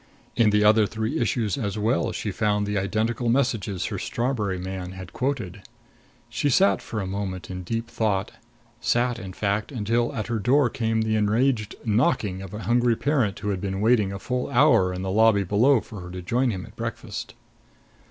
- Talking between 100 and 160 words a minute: No, average, 190 wpm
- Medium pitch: No, low, 110 Hz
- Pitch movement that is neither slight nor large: Yes, average, 3.4 semitones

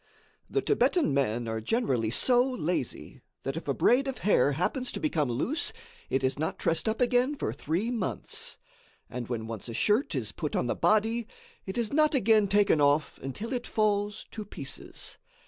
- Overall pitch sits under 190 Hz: No, high, 205 Hz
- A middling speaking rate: Yes, average, 180 wpm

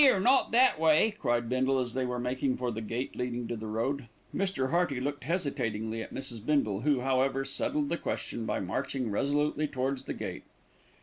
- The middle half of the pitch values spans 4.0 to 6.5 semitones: No, average, 3.6 semitones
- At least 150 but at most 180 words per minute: No, average, 190 wpm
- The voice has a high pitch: No, low, 130 Hz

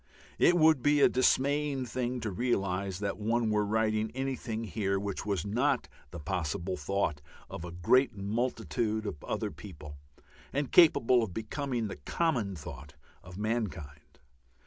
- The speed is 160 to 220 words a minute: No, average, 145 wpm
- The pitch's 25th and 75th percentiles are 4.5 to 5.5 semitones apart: Yes, average, 5.2 semitones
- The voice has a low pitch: Yes, low, 110 Hz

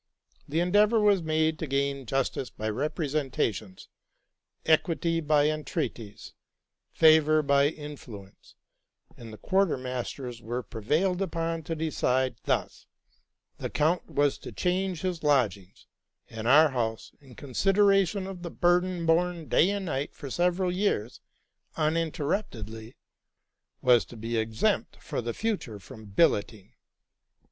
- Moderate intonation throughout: No, wide, 6.3 semitones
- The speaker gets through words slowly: Yes, slow, 125 wpm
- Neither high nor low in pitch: Yes, medium, 150 Hz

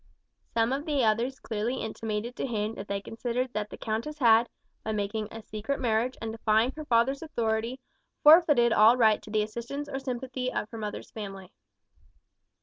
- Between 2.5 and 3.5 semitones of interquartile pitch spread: Yes, average, 3.0 semitones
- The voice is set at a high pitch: Yes, high, 230 Hz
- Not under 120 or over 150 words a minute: No, average, 175 wpm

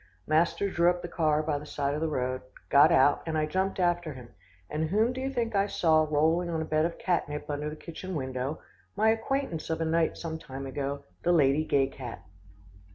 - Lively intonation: No, average, 3.3 semitones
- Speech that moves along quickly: Yes, fast, 225 wpm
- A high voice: No, medium, 160 Hz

